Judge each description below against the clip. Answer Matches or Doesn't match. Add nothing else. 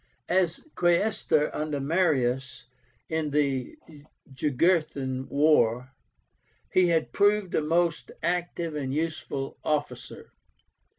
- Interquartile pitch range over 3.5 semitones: Matches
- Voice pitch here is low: Doesn't match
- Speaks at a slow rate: Matches